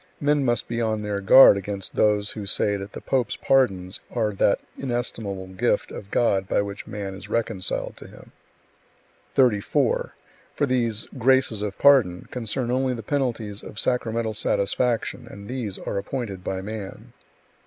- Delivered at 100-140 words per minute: No, average, 155 wpm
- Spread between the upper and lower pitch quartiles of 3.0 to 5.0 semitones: Yes, average, 3.7 semitones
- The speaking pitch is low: Yes, low, 110 Hz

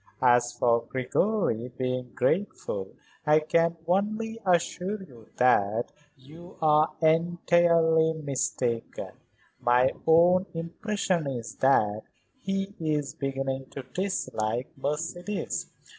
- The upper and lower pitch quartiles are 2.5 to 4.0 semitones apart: No, wide, 5.6 semitones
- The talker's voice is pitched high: No, medium, 155 Hz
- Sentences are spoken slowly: Yes, slow, 100 wpm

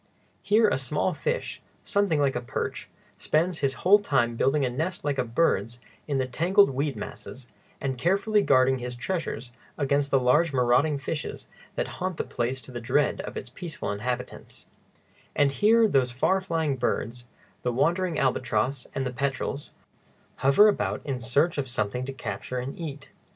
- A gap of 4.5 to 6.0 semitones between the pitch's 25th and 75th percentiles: Yes, average, 4.9 semitones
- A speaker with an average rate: Yes, average, 170 wpm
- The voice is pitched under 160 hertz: Yes, low, 135 Hz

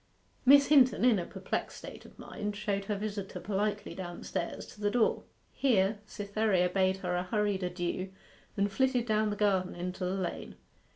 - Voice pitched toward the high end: Yes, high, 200 Hz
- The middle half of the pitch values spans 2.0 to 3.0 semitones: Yes, narrow, 2.4 semitones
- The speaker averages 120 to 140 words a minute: No, average, 170 wpm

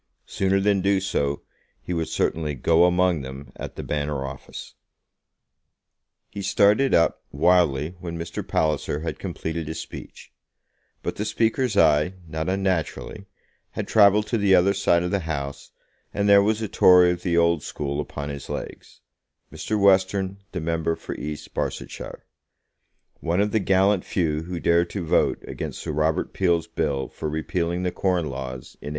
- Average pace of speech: Yes, average, 165 wpm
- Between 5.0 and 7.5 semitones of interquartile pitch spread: No, average, 3.9 semitones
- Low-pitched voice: Yes, very low, 85 Hz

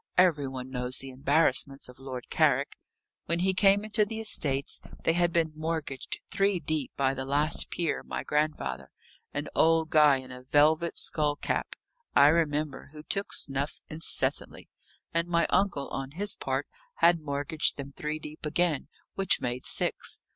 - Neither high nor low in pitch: Yes, medium, 150 Hz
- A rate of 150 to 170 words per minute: Yes, average, 160 wpm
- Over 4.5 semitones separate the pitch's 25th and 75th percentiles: No, average, 3.6 semitones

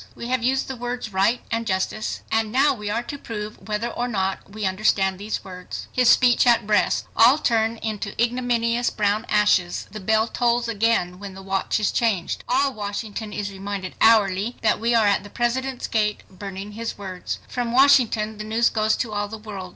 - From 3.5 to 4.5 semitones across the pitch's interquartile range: No, average, 2.7 semitones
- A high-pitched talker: Yes, high, 215 Hz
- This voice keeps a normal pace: Yes, average, 195 wpm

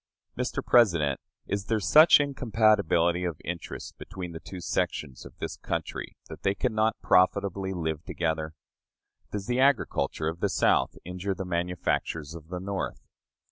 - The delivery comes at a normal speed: Yes, average, 150 wpm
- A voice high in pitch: No, very low, 90 Hz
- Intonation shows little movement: No, average, 3.9 semitones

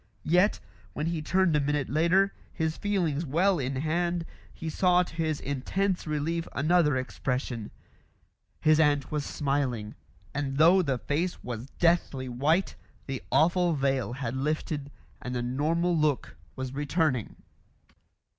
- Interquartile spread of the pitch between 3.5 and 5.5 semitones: Yes, average, 4.0 semitones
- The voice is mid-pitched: Yes, medium, 150 Hz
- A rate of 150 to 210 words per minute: No, slow, 135 wpm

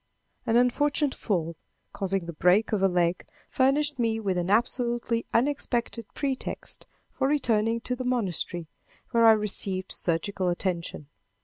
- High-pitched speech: Yes, high, 225 Hz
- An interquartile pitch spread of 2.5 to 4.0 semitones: No, average, 5.1 semitones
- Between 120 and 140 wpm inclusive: Yes, slow, 135 wpm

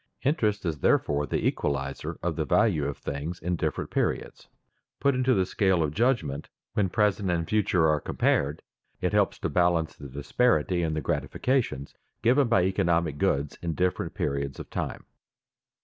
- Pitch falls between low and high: No, very low, 85 Hz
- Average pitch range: No, wide, 6.1 semitones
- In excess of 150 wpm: Yes, average, 165 wpm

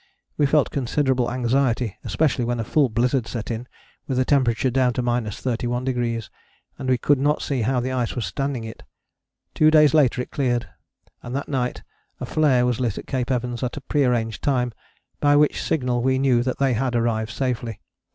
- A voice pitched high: No, low, 125 Hz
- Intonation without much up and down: Yes, narrow, 2.2 semitones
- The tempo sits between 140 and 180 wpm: No, average, 190 wpm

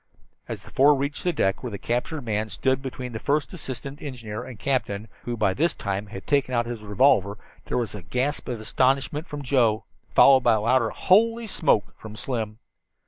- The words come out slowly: No, average, 200 wpm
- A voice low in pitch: Yes, low, 125 Hz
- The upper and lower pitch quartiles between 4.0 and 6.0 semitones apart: Yes, average, 4.3 semitones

